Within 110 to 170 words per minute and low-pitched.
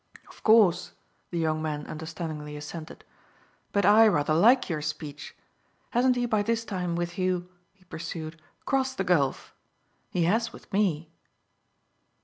No: average, 140 wpm; medium, 175 Hz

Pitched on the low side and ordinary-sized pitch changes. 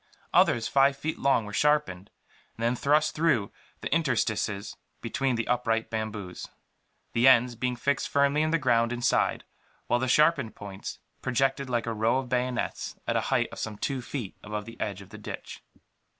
Yes: low, 120 Hz; average, 3.8 semitones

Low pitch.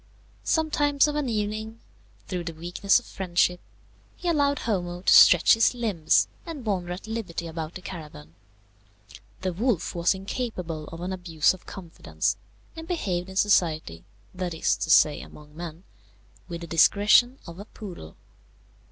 No: medium, 185 Hz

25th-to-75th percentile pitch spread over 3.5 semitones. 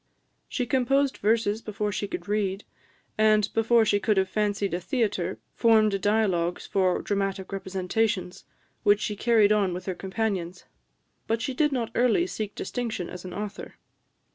No: average, 2.8 semitones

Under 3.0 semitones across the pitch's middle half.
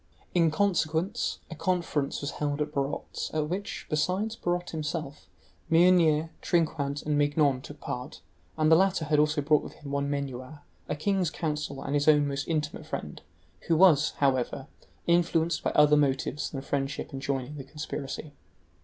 Yes: narrow, 2.6 semitones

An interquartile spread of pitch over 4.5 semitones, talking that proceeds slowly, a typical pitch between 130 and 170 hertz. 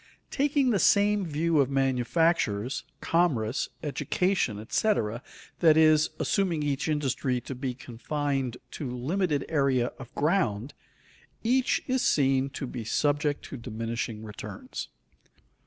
Yes: average, 5.2 semitones; slow, 120 wpm; medium, 140 Hz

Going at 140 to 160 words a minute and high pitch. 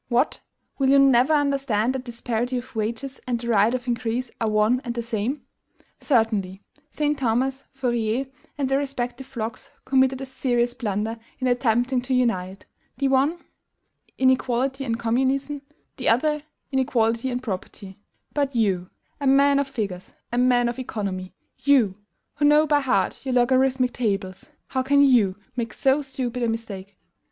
Yes: average, 155 wpm; very high, 250 Hz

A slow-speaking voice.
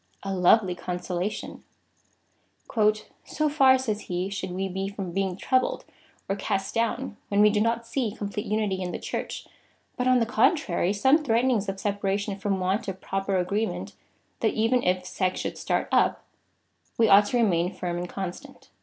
No: average, 170 wpm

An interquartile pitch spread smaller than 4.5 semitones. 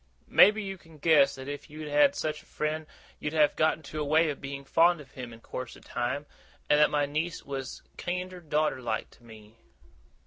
Yes: average, 2.8 semitones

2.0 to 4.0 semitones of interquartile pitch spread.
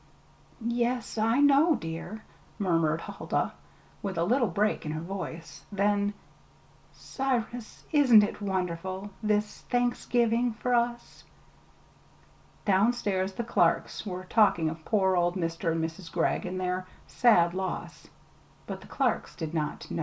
No: average, 5.2 semitones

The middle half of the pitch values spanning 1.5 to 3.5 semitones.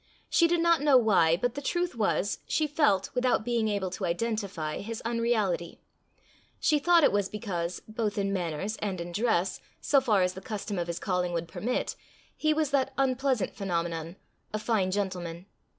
No: wide, 5.6 semitones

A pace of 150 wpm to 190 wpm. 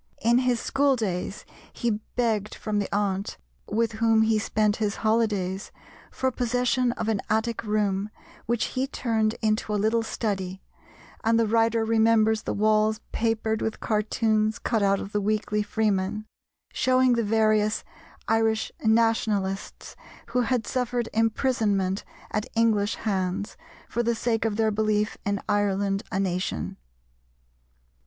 No: average, 140 wpm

